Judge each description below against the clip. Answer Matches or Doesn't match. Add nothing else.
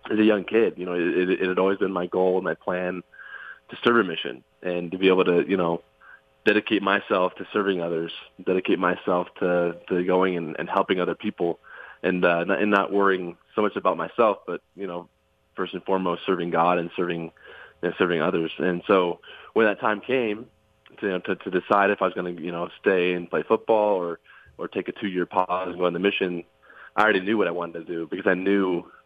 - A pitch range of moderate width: Doesn't match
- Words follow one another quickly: Matches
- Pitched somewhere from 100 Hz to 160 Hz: Doesn't match